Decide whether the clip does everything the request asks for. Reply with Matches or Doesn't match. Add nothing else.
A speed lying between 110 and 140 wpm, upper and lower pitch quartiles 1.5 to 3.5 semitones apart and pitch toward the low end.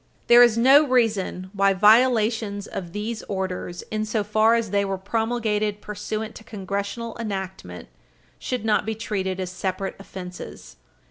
Doesn't match